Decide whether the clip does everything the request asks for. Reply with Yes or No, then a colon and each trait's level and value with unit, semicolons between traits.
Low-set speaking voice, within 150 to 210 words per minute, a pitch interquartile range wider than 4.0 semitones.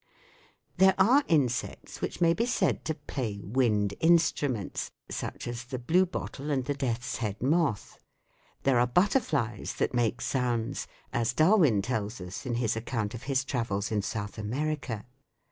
Yes: low, 125 Hz; average, 155 wpm; average, 5.2 semitones